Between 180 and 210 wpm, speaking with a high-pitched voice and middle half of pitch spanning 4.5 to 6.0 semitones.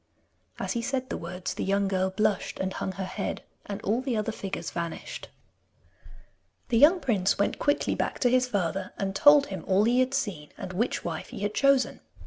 Yes: average, 200 wpm; high, 205 Hz; average, 5.0 semitones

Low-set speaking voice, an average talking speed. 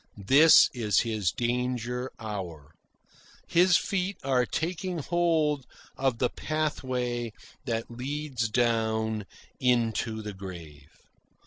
No: low, 125 Hz; slow, 100 wpm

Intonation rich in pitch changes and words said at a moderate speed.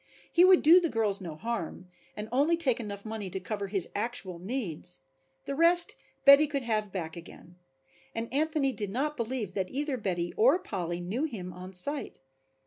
Yes: wide, 7.0 semitones; average, 175 wpm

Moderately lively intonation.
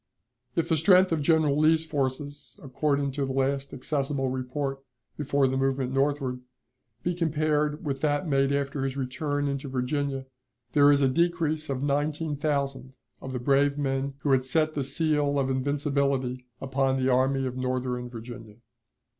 No: narrow, 1.9 semitones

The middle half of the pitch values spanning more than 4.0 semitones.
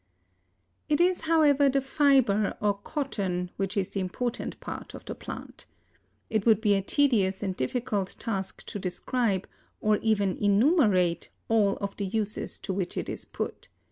Yes: average, 4.7 semitones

